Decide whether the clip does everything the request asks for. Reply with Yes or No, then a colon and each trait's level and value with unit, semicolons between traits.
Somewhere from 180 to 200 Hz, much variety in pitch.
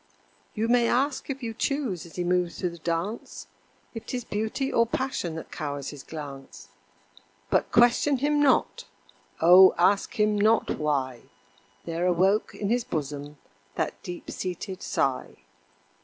Yes: high, 190 Hz; wide, 6.4 semitones